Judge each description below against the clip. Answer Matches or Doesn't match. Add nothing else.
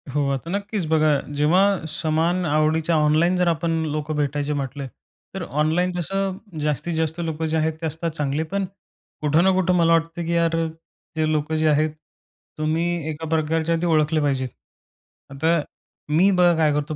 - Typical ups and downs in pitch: Doesn't match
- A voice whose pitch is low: Doesn't match